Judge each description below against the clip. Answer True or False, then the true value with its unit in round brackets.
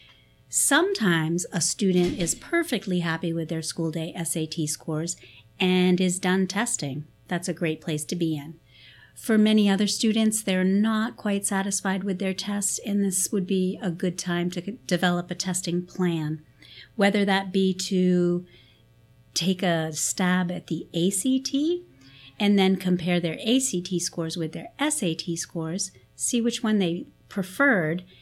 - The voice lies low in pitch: False (180 Hz)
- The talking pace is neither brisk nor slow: True (150 wpm)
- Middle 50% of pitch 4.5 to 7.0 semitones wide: False (3.3 semitones)